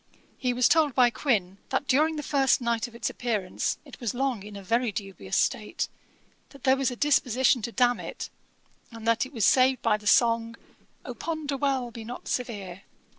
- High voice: Yes, high, 245 Hz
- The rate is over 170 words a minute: Yes, average, 195 wpm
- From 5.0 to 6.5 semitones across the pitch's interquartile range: No, average, 2.9 semitones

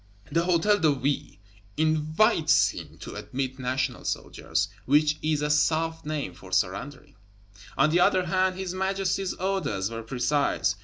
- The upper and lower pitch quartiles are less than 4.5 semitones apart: No, average, 4.9 semitones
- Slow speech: No, average, 145 wpm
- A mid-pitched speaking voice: Yes, medium, 155 Hz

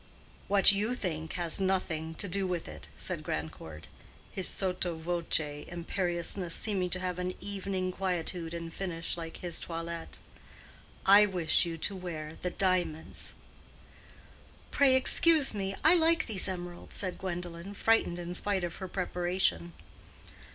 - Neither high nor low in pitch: Yes, medium, 180 Hz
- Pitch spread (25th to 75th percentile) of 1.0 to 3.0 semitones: Yes, narrow, 2.6 semitones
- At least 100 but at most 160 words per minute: Yes, average, 140 wpm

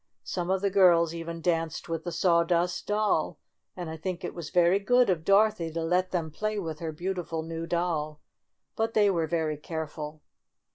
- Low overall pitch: No, medium, 170 Hz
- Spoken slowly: No, average, 185 wpm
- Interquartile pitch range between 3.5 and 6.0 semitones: No, narrow, 2.5 semitones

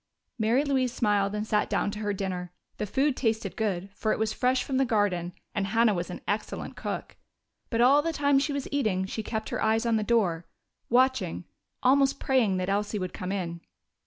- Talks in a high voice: Yes, high, 215 Hz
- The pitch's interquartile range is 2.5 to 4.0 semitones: No, average, 4.5 semitones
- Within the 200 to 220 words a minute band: Yes, fast, 205 wpm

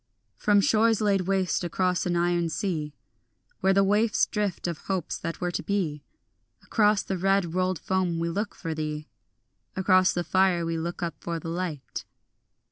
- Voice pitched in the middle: Yes, medium, 180 Hz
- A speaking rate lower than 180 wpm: Yes, average, 170 wpm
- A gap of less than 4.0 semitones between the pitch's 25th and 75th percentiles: Yes, average, 2.7 semitones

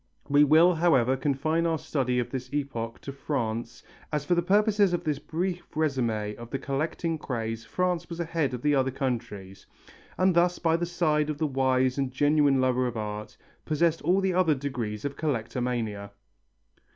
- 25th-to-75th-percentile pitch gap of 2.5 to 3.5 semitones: No, average, 4.8 semitones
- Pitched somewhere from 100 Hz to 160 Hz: Yes, medium, 140 Hz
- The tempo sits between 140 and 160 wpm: No, average, 175 wpm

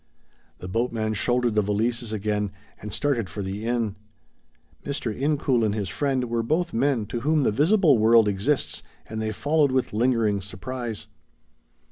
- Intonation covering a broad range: No, average, 3.8 semitones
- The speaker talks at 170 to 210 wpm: No, average, 155 wpm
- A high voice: No, low, 115 Hz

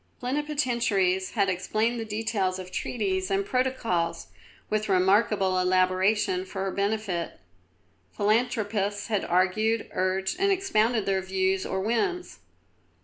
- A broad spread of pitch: No, average, 3.2 semitones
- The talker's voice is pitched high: Yes, high, 200 Hz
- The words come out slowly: Yes, slow, 115 wpm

